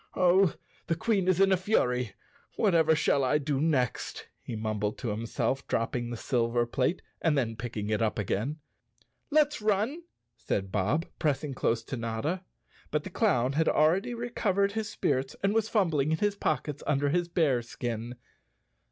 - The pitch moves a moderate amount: No, wide, 7.8 semitones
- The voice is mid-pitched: Yes, medium, 150 Hz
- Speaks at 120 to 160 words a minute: No, average, 170 wpm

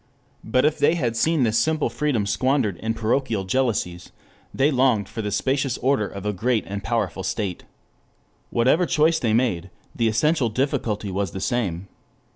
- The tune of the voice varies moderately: Yes, average, 4.7 semitones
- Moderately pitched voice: No, low, 115 Hz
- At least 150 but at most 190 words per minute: Yes, average, 165 wpm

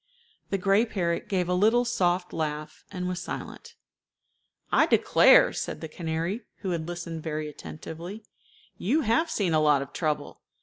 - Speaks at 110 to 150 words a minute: No, average, 160 wpm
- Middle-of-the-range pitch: Yes, medium, 175 Hz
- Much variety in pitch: No, average, 4.0 semitones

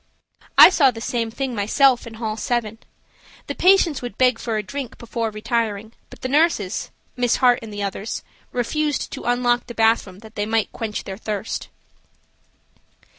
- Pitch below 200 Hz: No, high, 230 Hz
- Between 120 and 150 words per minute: No, average, 160 wpm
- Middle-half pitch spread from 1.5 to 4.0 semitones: Yes, narrow, 2.5 semitones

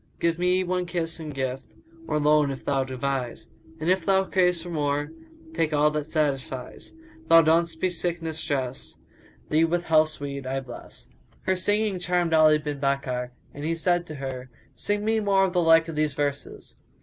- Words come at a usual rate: Yes, average, 195 wpm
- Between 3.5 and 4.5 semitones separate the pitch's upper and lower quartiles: Yes, average, 4.0 semitones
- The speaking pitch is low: No, medium, 160 Hz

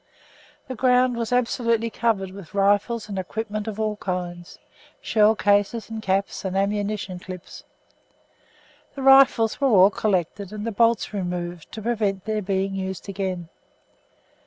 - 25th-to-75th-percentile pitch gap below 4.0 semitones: Yes, average, 2.9 semitones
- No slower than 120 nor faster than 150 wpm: Yes, average, 140 wpm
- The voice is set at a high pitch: Yes, high, 205 Hz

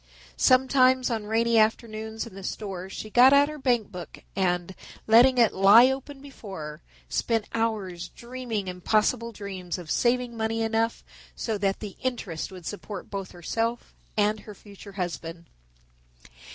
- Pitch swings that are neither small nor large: Yes, average, 3.8 semitones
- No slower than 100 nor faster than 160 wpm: Yes, average, 150 wpm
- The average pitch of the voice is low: No, high, 220 Hz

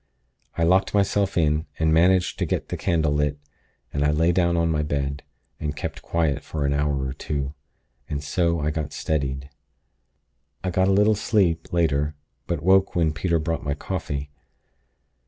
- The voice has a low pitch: Yes, very low, 80 Hz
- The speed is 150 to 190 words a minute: Yes, average, 175 wpm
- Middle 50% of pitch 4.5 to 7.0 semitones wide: No, average, 3.0 semitones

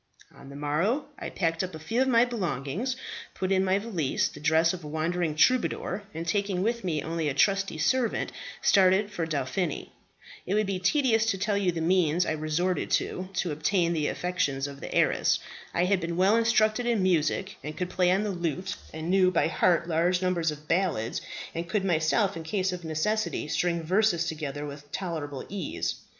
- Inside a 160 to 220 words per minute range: Yes, average, 195 wpm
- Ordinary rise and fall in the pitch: Yes, average, 3.7 semitones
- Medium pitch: Yes, medium, 180 Hz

